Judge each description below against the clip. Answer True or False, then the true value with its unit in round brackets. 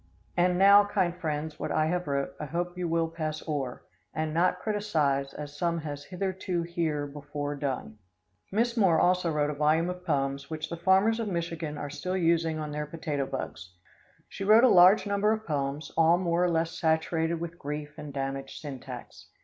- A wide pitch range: False (3.4 semitones)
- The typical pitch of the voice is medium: True (165 Hz)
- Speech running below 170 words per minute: False (190 wpm)